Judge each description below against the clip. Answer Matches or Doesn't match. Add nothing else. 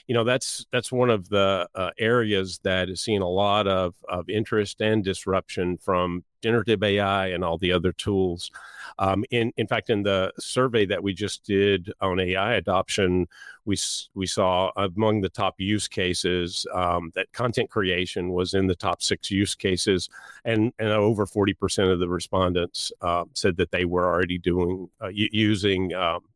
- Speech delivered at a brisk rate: Doesn't match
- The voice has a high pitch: Doesn't match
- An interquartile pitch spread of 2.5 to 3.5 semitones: Matches